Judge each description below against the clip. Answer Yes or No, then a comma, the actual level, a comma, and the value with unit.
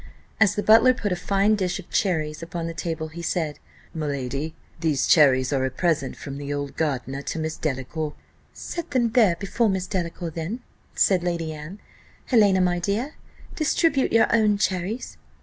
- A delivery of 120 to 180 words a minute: Yes, average, 170 wpm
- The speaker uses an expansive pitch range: No, average, 5.0 semitones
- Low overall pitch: No, medium, 170 Hz